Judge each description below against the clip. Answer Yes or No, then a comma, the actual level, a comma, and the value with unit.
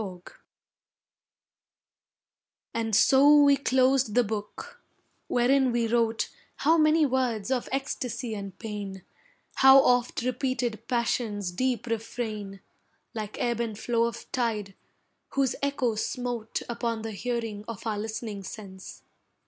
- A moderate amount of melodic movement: Yes, average, 3.0 semitones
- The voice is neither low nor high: No, high, 235 Hz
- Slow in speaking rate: Yes, slow, 120 wpm